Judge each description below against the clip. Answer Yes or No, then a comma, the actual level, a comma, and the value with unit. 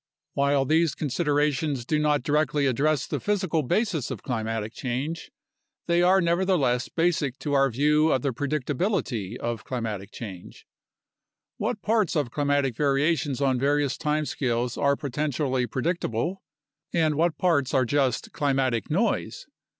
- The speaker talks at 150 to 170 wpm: No, average, 140 wpm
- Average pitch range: Yes, average, 3.9 semitones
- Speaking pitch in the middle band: Yes, medium, 145 Hz